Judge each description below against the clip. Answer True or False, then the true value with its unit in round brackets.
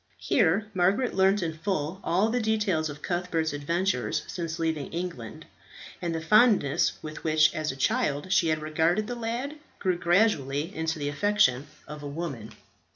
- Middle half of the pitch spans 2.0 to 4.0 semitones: False (4.6 semitones)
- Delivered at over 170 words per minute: False (160 wpm)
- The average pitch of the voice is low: False (165 Hz)